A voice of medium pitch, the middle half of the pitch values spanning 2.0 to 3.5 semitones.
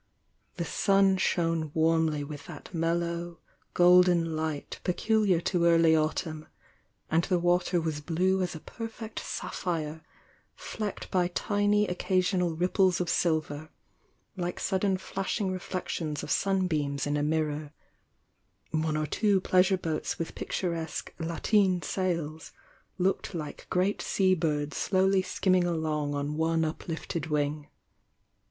Yes: medium, 170 Hz; average, 2.9 semitones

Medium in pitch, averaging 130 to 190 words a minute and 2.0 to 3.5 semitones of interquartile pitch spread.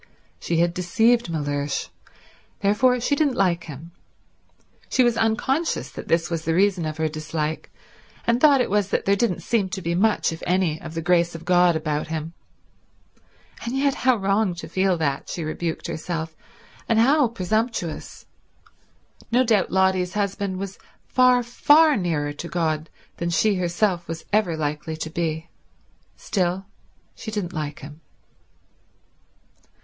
No: medium, 180 Hz; average, 155 wpm; average, 5.2 semitones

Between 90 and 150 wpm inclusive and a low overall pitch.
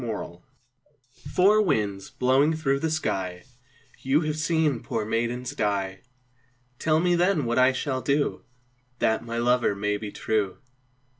Yes: average, 145 wpm; low, 125 Hz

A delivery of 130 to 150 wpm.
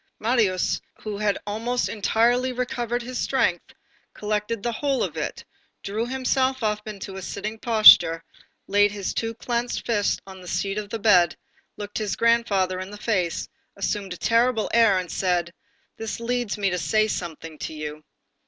No: average, 165 wpm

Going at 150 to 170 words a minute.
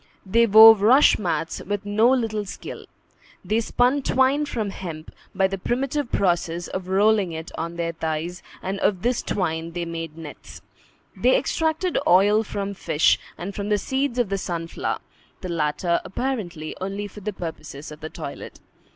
Yes: average, 165 wpm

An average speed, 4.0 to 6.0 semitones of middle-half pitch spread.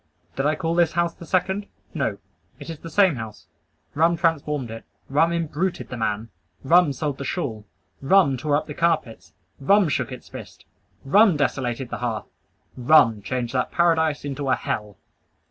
Yes: average, 170 wpm; average, 5.0 semitones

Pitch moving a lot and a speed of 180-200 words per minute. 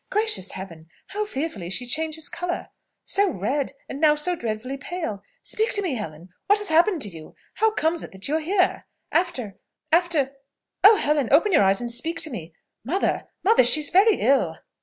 Yes: wide, 8.0 semitones; average, 185 wpm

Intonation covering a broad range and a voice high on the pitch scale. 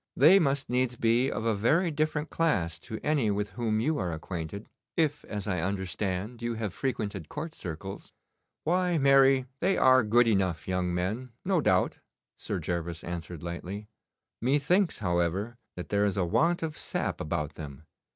No: wide, 7.3 semitones; low, 110 Hz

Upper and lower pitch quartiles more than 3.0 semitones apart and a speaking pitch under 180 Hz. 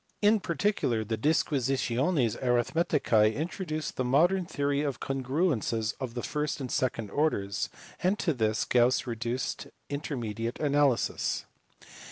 Yes: average, 4.7 semitones; low, 135 Hz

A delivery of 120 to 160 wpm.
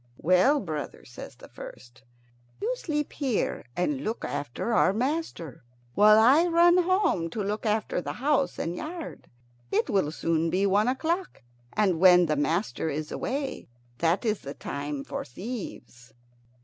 Yes: average, 150 wpm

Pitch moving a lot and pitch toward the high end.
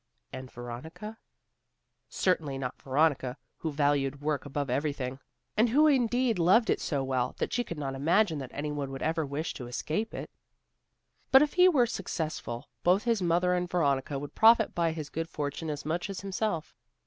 No: wide, 5.9 semitones; medium, 155 Hz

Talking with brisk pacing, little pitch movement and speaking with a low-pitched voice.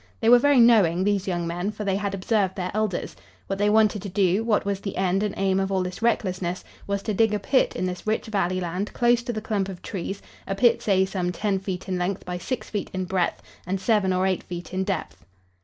No: fast, 245 wpm; narrow, 2.3 semitones; high, 195 Hz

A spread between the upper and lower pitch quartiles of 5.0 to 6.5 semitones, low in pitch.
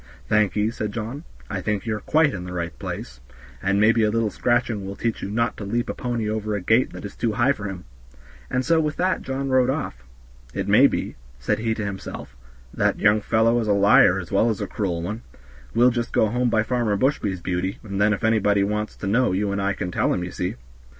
No: average, 3.2 semitones; low, 105 Hz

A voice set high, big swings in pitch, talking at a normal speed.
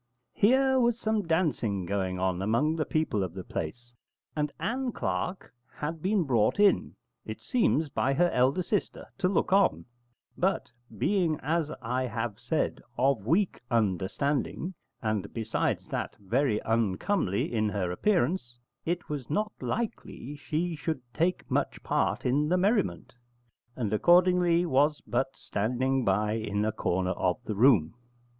No: low, 135 Hz; wide, 8.5 semitones; average, 145 wpm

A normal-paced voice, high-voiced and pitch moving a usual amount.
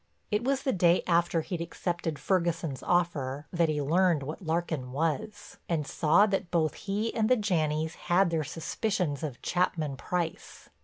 No: average, 160 wpm; medium, 170 Hz; average, 3.0 semitones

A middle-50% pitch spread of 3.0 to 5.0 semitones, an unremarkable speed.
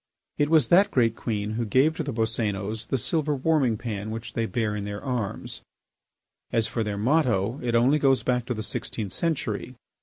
Yes: average, 3.9 semitones; average, 190 wpm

